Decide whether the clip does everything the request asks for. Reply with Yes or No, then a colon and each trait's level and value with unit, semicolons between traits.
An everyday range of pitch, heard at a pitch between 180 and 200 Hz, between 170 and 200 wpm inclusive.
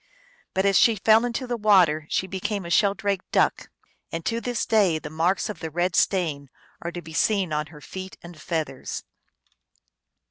Yes: average, 4.3 semitones; medium, 185 Hz; average, 180 wpm